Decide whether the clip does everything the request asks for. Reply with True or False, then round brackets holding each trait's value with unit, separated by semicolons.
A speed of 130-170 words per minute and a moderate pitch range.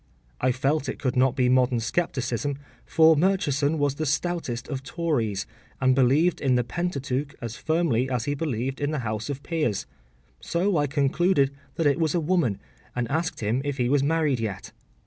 False (185 wpm; 4.1 semitones)